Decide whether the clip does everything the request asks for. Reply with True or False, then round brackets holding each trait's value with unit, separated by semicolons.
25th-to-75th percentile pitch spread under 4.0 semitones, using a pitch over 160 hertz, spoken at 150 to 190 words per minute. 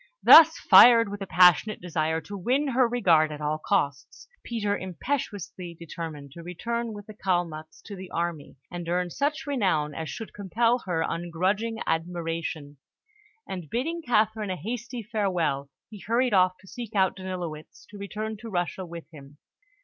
False (5.2 semitones; 185 Hz; 160 wpm)